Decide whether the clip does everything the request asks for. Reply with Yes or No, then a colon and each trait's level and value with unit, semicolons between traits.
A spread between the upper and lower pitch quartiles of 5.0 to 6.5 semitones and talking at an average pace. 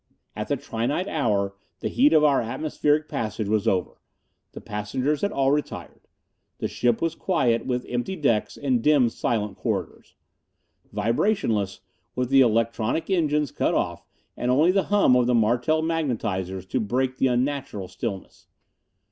Yes: average, 5.3 semitones; average, 150 wpm